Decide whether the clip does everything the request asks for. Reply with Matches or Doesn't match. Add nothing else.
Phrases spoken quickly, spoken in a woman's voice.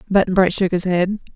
Matches